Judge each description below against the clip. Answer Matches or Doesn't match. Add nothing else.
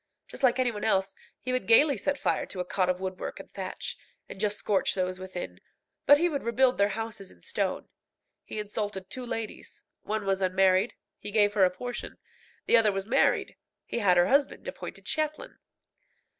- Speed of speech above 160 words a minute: Matches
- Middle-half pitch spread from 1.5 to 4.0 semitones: Doesn't match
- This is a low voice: Doesn't match